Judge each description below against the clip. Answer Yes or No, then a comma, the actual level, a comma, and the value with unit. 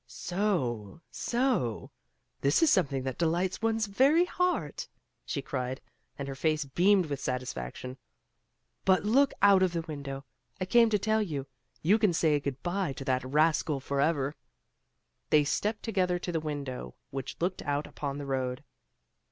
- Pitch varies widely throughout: Yes, wide, 6.2 semitones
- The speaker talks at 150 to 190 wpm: Yes, average, 155 wpm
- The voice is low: No, medium, 155 Hz